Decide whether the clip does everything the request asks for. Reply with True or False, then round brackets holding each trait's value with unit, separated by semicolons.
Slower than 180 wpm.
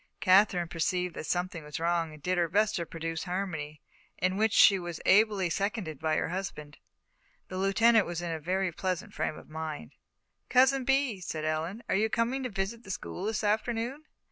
False (190 wpm)